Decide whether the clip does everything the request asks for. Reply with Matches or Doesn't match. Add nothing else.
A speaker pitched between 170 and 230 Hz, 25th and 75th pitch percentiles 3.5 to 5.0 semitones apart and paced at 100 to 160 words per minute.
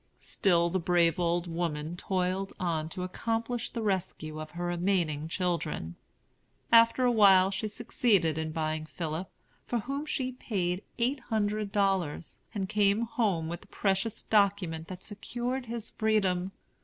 Matches